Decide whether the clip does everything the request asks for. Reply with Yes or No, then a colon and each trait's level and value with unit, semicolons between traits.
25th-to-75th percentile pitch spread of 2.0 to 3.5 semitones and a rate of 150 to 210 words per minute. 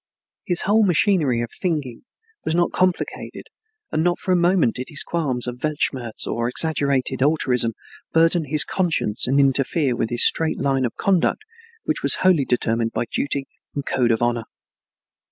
No: wide, 5.6 semitones; average, 160 wpm